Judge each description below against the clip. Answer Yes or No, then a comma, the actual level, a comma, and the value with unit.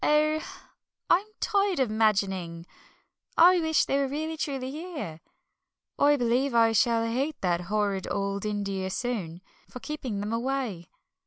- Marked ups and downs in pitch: Yes, wide, 6.7 semitones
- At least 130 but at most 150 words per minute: Yes, average, 140 wpm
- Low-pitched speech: No, high, 235 Hz